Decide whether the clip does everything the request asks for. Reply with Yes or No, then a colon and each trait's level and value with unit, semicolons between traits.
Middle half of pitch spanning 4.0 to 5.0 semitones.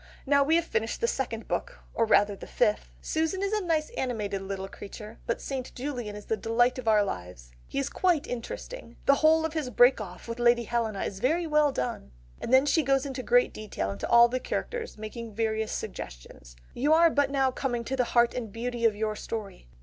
Yes: average, 4.7 semitones